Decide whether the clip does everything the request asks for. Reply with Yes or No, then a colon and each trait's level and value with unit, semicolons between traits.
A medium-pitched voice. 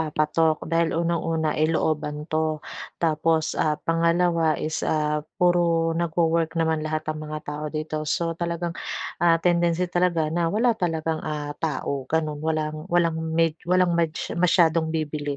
Yes: medium, 160 Hz